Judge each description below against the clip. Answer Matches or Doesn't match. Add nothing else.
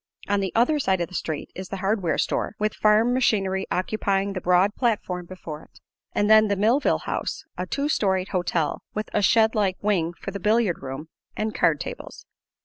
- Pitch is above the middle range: Matches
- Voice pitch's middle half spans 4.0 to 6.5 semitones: Doesn't match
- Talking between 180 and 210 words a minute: Matches